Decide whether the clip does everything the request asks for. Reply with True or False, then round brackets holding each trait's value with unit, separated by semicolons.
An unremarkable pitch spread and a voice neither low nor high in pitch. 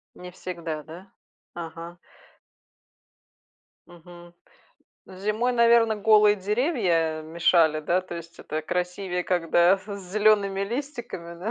True (3.9 semitones; 180 Hz)